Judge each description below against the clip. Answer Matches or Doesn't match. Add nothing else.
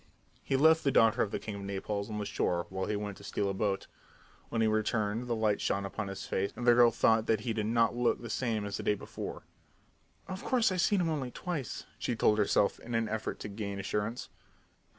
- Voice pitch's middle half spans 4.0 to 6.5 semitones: Doesn't match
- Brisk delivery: Matches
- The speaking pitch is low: Matches